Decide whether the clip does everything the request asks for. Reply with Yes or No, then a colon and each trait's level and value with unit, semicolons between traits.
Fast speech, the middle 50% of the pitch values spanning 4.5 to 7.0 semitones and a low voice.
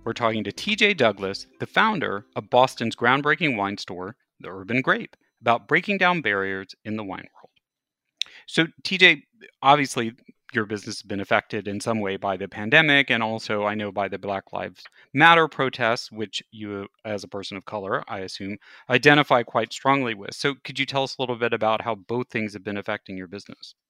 No: average, 195 wpm; average, 5.1 semitones; low, 115 Hz